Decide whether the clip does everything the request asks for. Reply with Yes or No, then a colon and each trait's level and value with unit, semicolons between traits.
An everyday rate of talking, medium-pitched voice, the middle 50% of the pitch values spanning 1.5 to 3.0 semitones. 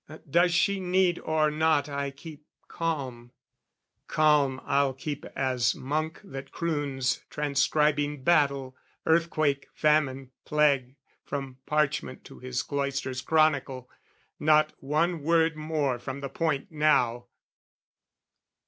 No: slow, 110 wpm; medium, 145 Hz; narrow, 2.6 semitones